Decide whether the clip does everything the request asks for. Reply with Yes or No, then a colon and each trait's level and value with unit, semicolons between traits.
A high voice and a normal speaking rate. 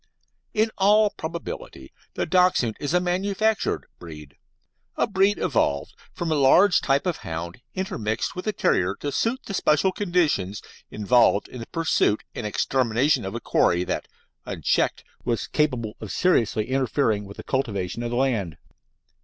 No: low, 130 Hz; average, 155 wpm